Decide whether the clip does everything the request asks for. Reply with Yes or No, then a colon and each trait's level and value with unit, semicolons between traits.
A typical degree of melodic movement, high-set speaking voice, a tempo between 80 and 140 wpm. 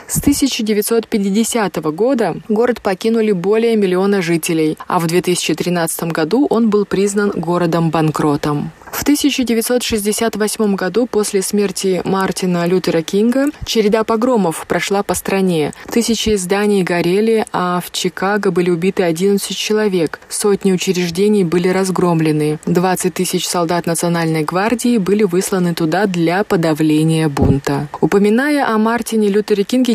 Yes: average, 3.6 semitones; high, 195 Hz; average, 120 wpm